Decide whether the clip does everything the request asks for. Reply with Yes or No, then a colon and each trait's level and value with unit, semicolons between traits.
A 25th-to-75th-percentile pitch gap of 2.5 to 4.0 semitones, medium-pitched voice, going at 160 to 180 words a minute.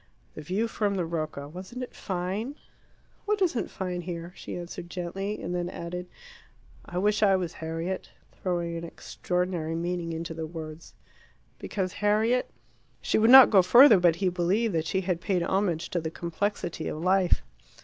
Yes: average, 2.9 semitones; medium, 180 Hz; average, 170 wpm